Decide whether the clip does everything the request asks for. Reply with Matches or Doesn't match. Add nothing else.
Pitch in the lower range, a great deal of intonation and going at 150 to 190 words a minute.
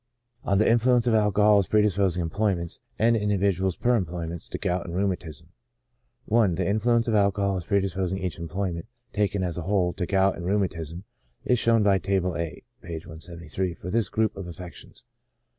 Doesn't match